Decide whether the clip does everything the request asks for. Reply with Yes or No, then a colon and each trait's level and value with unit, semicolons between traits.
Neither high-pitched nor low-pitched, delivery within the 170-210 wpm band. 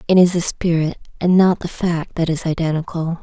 Yes: medium, 170 Hz; fast, 205 wpm